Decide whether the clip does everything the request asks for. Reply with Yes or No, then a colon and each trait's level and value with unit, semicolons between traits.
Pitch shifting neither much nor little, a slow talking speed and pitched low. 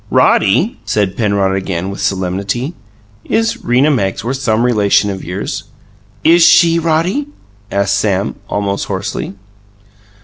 No: wide, 7.2 semitones; slow, 115 wpm; low, 105 Hz